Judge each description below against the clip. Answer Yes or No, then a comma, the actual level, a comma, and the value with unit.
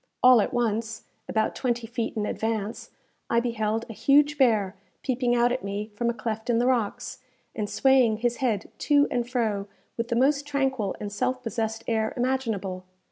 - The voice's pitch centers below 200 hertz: No, high, 235 Hz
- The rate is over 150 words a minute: Yes, average, 180 wpm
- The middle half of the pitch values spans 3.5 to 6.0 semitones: No, narrow, 2.6 semitones